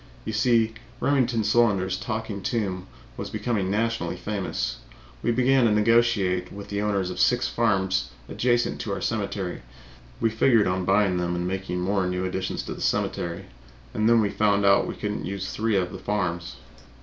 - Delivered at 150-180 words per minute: Yes, average, 175 wpm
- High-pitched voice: No, low, 100 Hz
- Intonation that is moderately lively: Yes, average, 3.4 semitones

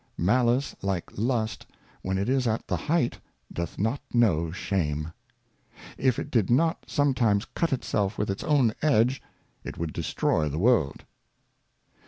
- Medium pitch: No, low, 110 Hz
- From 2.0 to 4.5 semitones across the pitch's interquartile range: No, average, 5.3 semitones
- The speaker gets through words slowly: No, average, 145 wpm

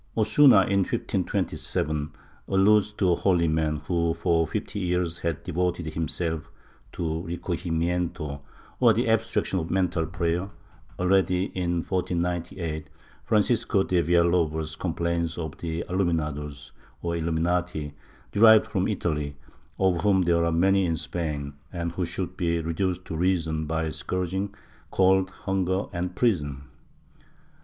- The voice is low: Yes, very low, 85 Hz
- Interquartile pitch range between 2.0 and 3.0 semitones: Yes, narrow, 2.5 semitones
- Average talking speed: No, slow, 130 wpm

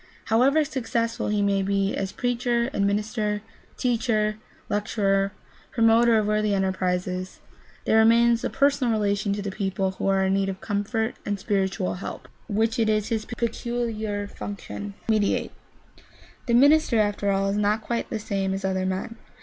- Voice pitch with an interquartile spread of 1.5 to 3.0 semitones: Yes, narrow, 2.6 semitones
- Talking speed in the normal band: Yes, average, 155 wpm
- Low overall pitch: No, high, 210 Hz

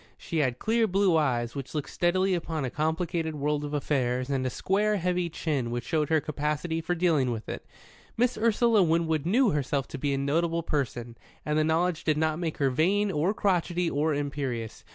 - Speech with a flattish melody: No, average, 3.9 semitones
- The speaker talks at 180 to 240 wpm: Yes, average, 195 wpm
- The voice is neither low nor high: Yes, medium, 155 Hz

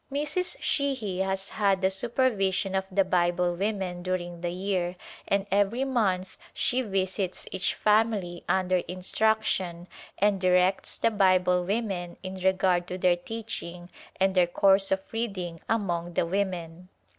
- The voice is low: No, high, 190 Hz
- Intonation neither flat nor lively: No, narrow, 2.2 semitones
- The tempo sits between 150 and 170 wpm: No, average, 140 wpm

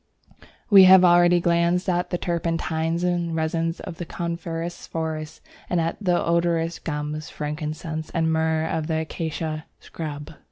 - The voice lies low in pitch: No, medium, 165 Hz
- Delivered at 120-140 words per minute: Yes, slow, 135 wpm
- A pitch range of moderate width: No, narrow, 1.5 semitones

